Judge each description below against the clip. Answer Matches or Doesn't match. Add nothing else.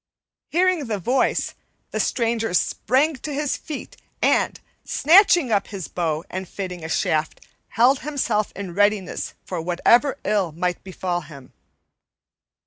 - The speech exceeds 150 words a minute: Doesn't match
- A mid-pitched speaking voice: Doesn't match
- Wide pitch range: Matches